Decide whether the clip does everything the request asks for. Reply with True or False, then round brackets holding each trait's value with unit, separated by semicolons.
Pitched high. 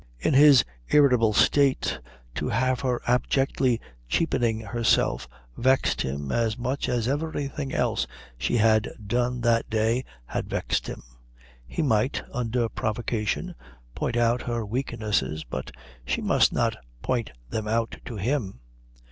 False (120 Hz)